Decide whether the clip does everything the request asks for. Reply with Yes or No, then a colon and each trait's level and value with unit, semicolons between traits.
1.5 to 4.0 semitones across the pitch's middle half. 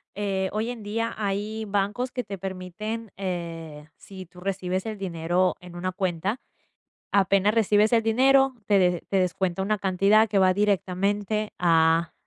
Yes: average, 2.7 semitones